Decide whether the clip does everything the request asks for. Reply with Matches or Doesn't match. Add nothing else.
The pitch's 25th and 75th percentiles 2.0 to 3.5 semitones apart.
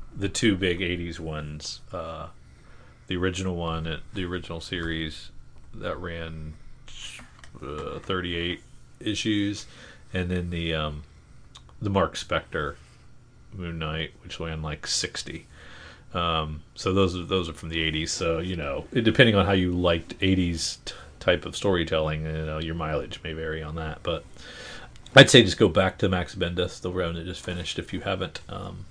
Matches